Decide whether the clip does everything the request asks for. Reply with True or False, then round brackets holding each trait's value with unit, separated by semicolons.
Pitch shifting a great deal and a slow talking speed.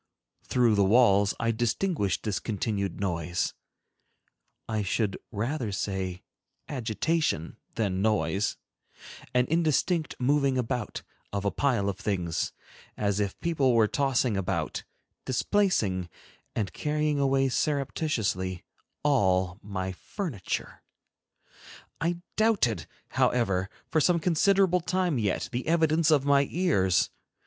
True (7.4 semitones; 105 wpm)